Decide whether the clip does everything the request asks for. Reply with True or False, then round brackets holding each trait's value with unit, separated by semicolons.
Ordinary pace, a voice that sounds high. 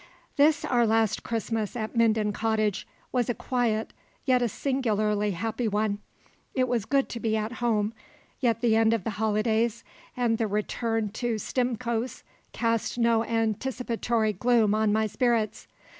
True (150 wpm; 225 Hz)